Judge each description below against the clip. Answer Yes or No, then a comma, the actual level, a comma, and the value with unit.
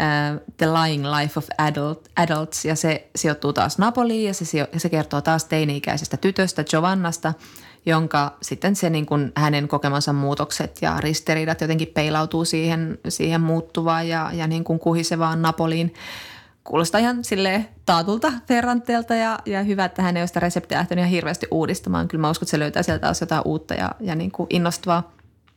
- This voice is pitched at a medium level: Yes, medium, 165 Hz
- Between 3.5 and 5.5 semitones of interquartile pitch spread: No, narrow, 2.6 semitones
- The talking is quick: Yes, fast, 175 wpm